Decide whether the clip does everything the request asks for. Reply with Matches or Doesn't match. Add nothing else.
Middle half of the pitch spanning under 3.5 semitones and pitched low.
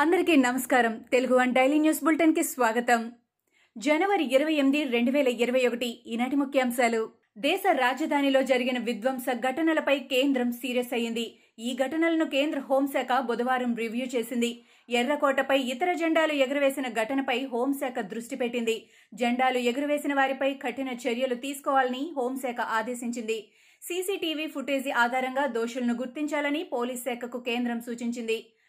Doesn't match